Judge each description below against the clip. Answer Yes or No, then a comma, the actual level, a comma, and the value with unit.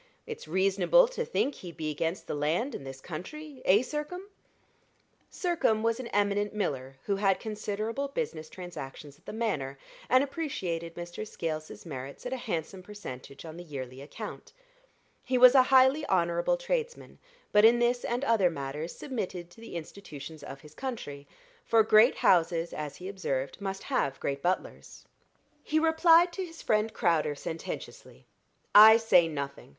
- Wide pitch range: Yes, wide, 8.1 semitones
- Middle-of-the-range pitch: No, high, 195 Hz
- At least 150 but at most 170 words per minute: Yes, average, 160 wpm